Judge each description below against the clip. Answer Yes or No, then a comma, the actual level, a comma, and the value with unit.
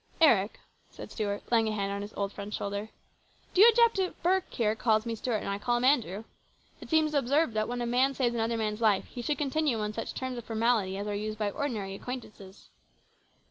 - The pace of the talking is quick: Yes, fast, 230 wpm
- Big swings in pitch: No, average, 3.7 semitones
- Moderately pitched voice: No, high, 225 Hz